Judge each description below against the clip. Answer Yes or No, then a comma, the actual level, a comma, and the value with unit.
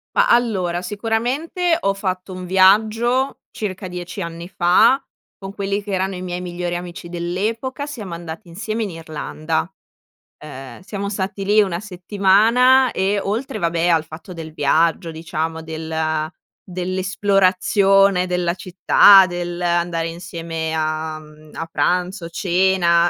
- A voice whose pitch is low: No, medium, 180 Hz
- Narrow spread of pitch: No, average, 3.0 semitones